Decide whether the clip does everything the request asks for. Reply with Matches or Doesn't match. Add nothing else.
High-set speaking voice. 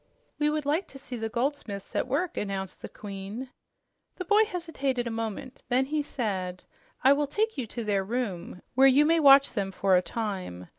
Matches